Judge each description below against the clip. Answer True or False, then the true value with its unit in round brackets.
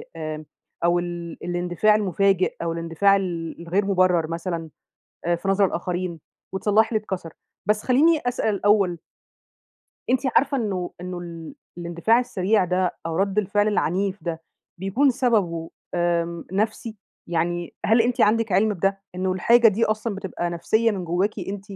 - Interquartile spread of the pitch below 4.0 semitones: True (3.5 semitones)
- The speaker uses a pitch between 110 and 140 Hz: False (190 Hz)